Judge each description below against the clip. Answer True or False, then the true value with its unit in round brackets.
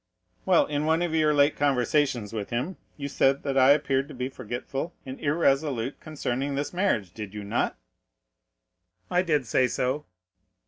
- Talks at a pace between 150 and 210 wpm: True (165 wpm)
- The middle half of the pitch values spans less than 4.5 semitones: True (3.2 semitones)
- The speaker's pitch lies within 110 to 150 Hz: True (140 Hz)